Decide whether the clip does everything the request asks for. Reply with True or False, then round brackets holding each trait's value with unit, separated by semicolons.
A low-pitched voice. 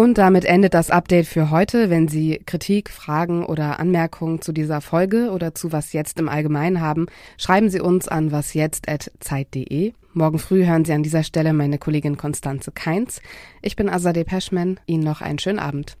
False (165 Hz)